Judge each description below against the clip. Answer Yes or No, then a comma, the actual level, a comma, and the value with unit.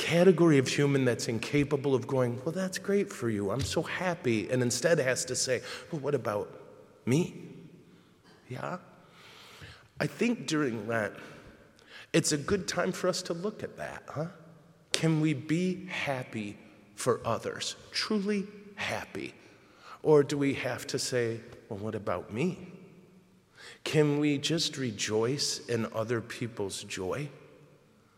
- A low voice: No, medium, 145 Hz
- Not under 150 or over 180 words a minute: No, average, 140 wpm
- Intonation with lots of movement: Yes, wide, 6.6 semitones